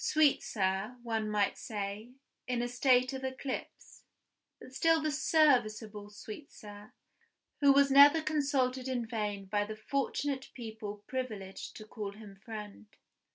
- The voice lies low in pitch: No, high, 235 Hz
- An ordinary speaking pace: No, slow, 130 wpm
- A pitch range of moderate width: Yes, average, 4.3 semitones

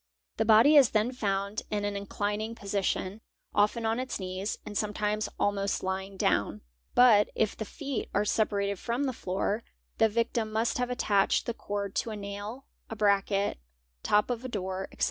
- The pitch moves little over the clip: Yes, narrow, 2.3 semitones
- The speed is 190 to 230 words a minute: No, average, 180 wpm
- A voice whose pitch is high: Yes, high, 210 Hz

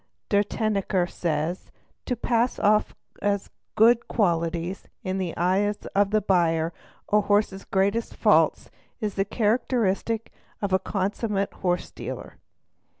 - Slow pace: Yes, slow, 130 wpm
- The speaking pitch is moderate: No, high, 200 Hz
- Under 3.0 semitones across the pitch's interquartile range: Yes, narrow, 2.5 semitones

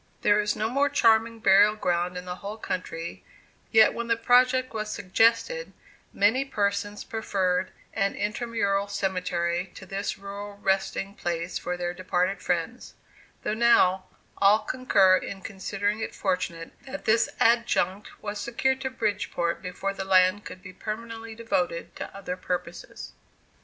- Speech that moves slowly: No, average, 145 wpm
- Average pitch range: Yes, average, 3.4 semitones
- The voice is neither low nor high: No, high, 200 Hz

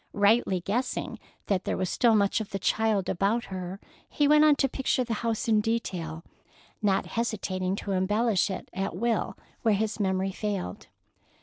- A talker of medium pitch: No, high, 205 Hz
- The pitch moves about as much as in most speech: Yes, average, 3.3 semitones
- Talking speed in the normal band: Yes, average, 170 wpm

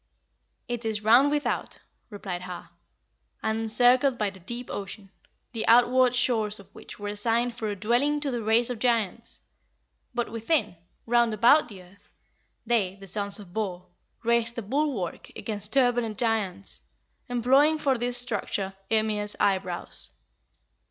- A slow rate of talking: No, average, 145 wpm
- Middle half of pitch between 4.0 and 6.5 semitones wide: No, average, 3.1 semitones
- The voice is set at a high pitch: Yes, high, 225 Hz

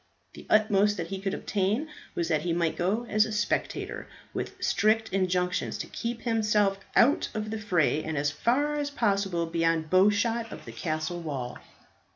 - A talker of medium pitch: No, high, 195 Hz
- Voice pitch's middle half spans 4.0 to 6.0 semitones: Yes, average, 4.3 semitones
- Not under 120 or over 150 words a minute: No, average, 180 wpm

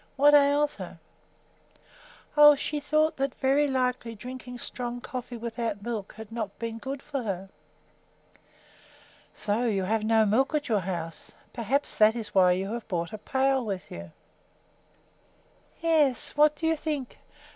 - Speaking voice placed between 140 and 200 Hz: No, high, 240 Hz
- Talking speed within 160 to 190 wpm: No, average, 150 wpm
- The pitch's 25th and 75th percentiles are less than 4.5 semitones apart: No, average, 4.8 semitones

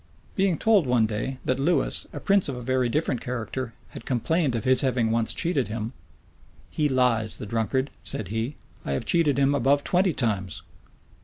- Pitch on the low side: Yes, low, 130 Hz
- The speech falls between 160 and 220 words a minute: Yes, average, 180 wpm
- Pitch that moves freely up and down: No, average, 4.1 semitones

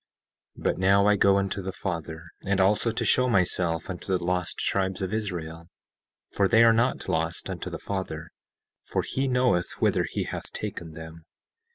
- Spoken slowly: No, average, 180 wpm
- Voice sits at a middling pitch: No, very low, 95 Hz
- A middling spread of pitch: Yes, average, 3.3 semitones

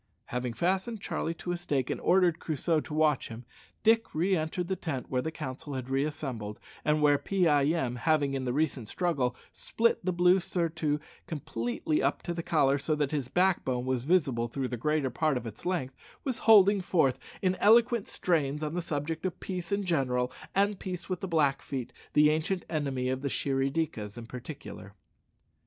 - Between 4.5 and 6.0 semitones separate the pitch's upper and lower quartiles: Yes, average, 5.1 semitones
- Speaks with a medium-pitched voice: Yes, medium, 150 Hz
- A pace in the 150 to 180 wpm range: No, average, 190 wpm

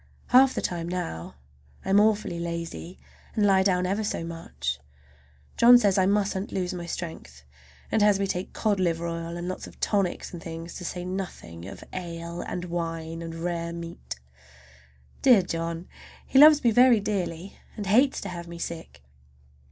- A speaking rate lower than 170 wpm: No, average, 175 wpm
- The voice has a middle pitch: Yes, medium, 180 Hz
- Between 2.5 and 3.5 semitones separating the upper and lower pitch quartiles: Yes, average, 3.1 semitones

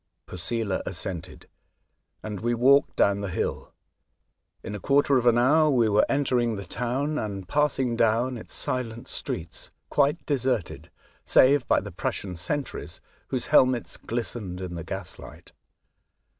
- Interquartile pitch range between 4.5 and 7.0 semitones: Yes, average, 4.9 semitones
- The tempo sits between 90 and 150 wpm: Yes, average, 140 wpm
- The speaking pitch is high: No, low, 120 Hz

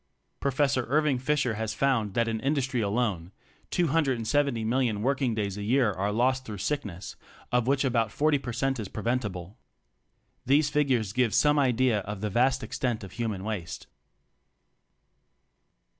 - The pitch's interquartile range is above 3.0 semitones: Yes, average, 4.2 semitones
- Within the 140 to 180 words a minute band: Yes, average, 145 wpm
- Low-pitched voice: Yes, low, 120 Hz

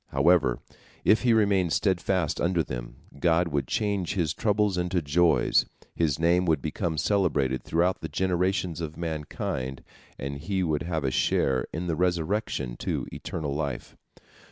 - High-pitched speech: No, very low, 85 Hz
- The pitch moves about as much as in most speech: Yes, average, 4.0 semitones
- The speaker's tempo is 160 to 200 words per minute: No, average, 150 wpm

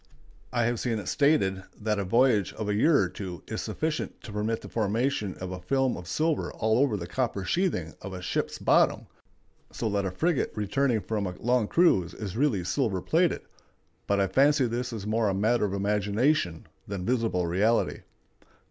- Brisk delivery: No, average, 190 wpm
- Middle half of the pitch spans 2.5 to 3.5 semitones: No, average, 4.6 semitones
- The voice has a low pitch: Yes, low, 105 Hz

